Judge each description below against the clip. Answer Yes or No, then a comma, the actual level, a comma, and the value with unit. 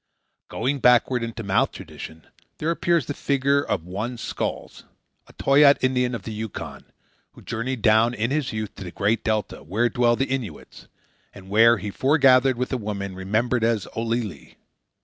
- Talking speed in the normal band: Yes, average, 170 wpm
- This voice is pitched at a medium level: No, low, 115 Hz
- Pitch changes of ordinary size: Yes, average, 3.5 semitones